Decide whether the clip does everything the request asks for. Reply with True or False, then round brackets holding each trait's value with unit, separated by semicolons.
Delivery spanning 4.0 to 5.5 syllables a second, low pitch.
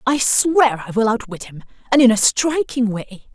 False (4.5 syllables/s; 235 Hz)